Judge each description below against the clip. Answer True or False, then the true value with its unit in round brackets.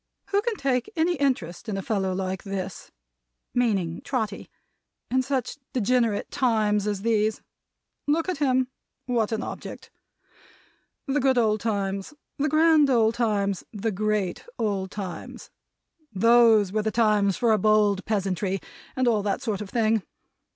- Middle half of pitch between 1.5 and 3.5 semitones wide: False (4.0 semitones)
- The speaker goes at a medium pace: True (145 wpm)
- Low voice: False (220 Hz)